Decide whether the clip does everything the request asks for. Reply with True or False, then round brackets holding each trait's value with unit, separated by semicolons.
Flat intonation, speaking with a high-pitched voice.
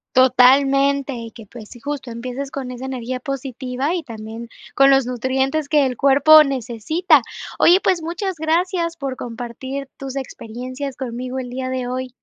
True (2.1 semitones; 265 Hz)